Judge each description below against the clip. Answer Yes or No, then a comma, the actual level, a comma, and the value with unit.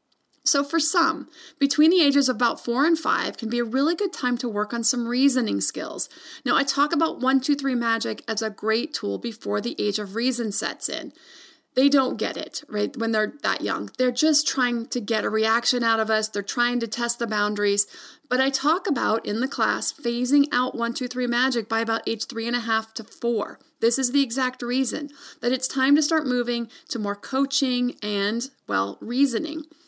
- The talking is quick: Yes, fast, 215 wpm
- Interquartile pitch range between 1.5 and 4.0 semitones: Yes, average, 3.7 semitones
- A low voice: No, high, 245 Hz